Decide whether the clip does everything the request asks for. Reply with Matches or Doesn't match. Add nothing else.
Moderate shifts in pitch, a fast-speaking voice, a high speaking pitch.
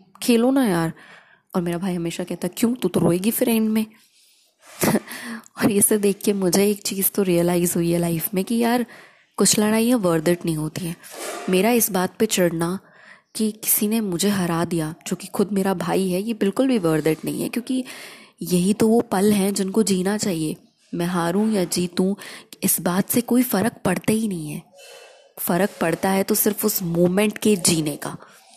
Matches